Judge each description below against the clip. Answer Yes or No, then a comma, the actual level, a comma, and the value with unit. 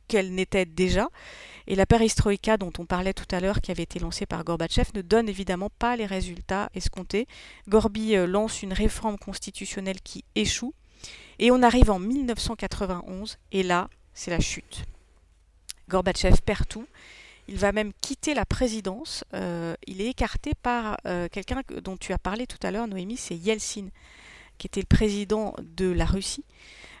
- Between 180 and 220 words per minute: No, average, 165 wpm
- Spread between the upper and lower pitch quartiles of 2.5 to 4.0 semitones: Yes, average, 2.9 semitones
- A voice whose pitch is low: No, high, 195 Hz